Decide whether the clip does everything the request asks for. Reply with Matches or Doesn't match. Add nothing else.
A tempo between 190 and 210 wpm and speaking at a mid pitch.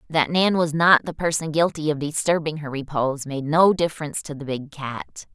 Matches